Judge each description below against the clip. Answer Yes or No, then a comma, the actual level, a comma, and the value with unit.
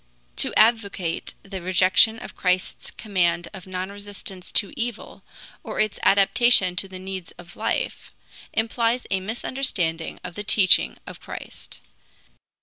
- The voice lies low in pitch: No, high, 195 Hz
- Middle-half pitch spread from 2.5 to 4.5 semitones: Yes, average, 3.1 semitones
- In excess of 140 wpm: No, slow, 135 wpm